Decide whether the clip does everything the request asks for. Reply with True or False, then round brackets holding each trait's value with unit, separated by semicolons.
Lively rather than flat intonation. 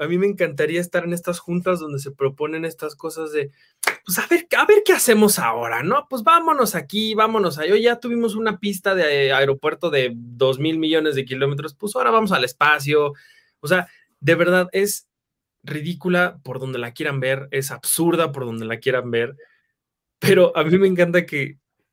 True (6.0 semitones)